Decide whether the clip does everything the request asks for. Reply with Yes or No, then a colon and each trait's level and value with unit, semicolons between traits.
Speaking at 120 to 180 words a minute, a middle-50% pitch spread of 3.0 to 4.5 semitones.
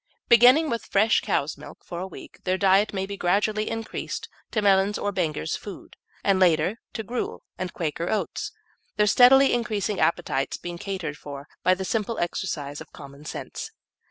Yes: average, 165 wpm; average, 3.9 semitones